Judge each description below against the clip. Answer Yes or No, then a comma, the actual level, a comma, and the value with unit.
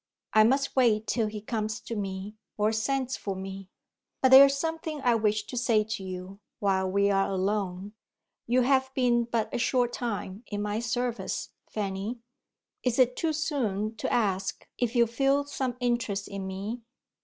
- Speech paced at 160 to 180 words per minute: Yes, average, 175 wpm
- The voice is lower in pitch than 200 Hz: No, high, 220 Hz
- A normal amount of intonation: Yes, average, 3.9 semitones